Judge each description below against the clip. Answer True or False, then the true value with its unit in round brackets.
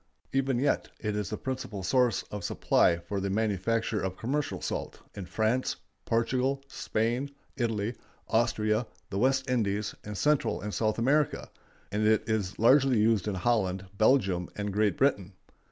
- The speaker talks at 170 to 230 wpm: False (155 wpm)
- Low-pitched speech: True (110 Hz)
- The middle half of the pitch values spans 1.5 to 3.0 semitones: False (3.8 semitones)